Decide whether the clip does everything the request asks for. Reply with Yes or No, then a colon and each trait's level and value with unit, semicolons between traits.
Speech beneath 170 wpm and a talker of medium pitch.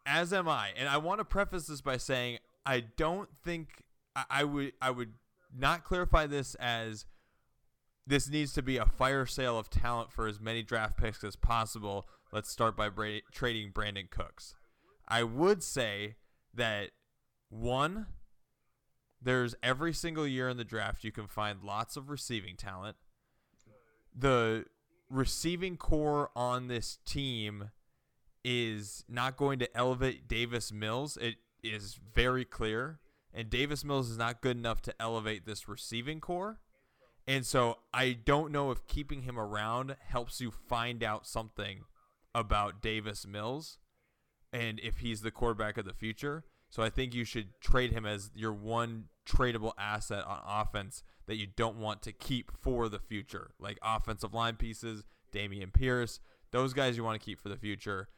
No: average, 160 wpm; low, 115 Hz